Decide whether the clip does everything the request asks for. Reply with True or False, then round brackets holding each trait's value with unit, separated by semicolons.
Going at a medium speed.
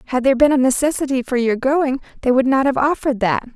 False (235 wpm)